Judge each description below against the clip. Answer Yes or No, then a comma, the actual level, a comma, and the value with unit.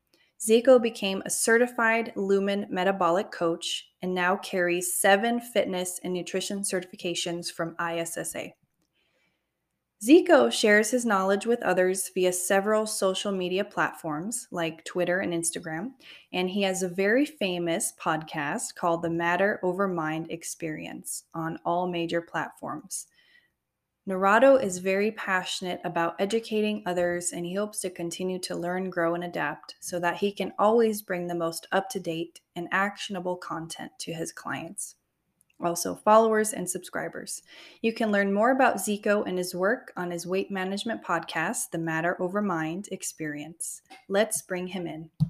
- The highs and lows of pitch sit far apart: No, average, 3.3 semitones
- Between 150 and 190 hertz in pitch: Yes, medium, 185 Hz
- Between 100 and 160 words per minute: Yes, average, 145 wpm